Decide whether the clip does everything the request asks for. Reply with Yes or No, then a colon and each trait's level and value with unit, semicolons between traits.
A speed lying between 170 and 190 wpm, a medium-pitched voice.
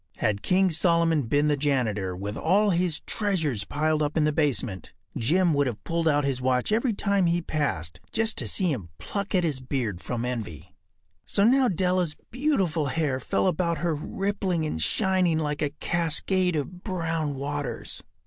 Yes: average, 175 wpm; medium, 155 Hz